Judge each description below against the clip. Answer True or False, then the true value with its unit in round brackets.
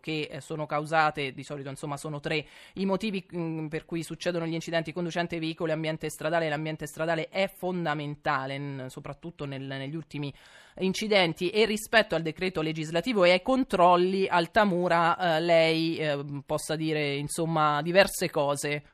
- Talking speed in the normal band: True (150 wpm)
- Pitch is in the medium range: True (160 Hz)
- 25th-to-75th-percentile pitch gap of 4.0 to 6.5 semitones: False (2.9 semitones)